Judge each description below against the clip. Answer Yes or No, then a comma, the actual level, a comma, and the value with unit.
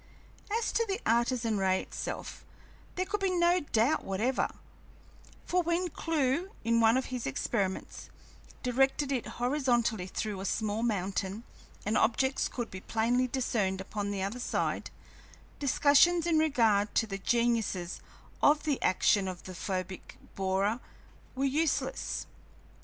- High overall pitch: Yes, high, 235 Hz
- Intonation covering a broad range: Yes, wide, 6.1 semitones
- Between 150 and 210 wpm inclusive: No, slow, 135 wpm